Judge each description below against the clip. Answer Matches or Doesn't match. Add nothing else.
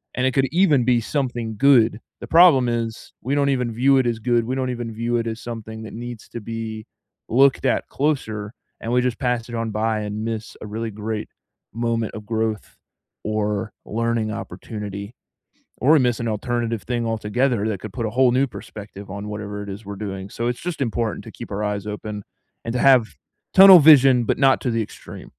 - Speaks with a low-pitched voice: Matches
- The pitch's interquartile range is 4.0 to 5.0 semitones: Doesn't match